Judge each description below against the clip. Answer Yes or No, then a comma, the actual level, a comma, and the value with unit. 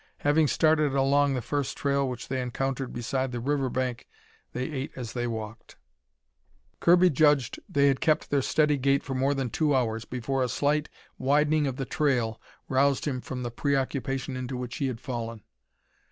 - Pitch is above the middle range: No, low, 135 Hz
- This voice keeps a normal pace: Yes, average, 180 wpm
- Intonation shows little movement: Yes, narrow, 2.3 semitones